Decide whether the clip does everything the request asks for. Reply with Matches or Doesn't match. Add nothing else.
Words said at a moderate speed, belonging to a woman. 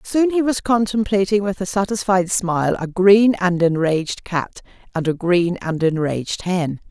Matches